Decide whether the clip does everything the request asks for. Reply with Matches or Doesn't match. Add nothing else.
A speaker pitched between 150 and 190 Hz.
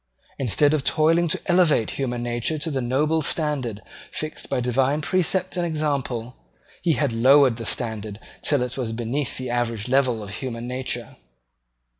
Doesn't match